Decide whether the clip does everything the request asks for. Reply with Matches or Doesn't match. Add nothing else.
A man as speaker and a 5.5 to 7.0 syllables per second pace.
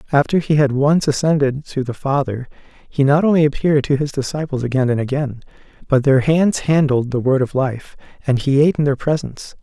Matches